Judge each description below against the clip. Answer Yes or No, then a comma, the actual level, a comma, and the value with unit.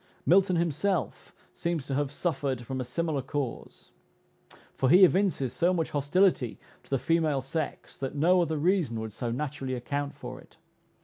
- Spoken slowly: No, average, 165 wpm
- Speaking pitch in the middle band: Yes, medium, 145 Hz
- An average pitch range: Yes, average, 4.4 semitones